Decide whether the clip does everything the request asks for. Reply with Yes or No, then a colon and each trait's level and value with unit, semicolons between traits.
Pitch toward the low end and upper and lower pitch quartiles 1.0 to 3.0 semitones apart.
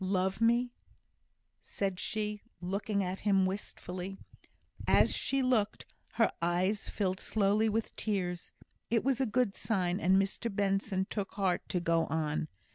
No: high, 195 Hz; average, 2.7 semitones